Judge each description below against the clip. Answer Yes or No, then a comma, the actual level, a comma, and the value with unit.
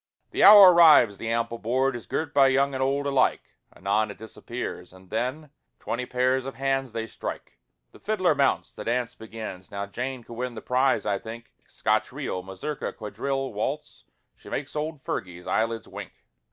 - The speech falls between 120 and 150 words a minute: No, average, 180 wpm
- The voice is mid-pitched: No, low, 125 Hz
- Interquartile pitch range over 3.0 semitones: Yes, average, 3.6 semitones